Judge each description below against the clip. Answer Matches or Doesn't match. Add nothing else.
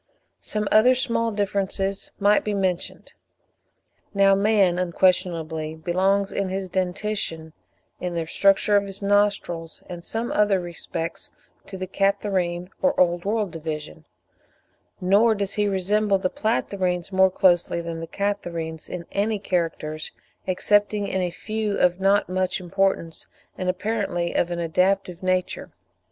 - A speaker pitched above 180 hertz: Matches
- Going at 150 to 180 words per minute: Doesn't match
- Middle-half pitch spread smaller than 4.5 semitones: Matches